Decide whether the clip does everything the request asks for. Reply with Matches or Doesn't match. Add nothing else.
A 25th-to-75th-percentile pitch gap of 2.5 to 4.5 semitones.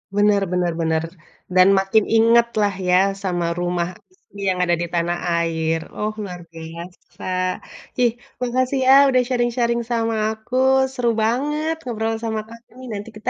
Doesn't match